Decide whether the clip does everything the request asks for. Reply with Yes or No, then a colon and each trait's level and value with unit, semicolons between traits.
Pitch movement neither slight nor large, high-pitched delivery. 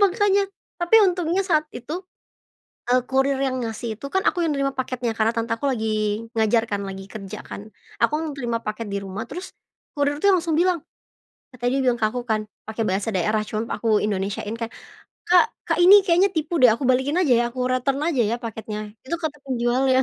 No: wide, 6.3 semitones; very high, 250 Hz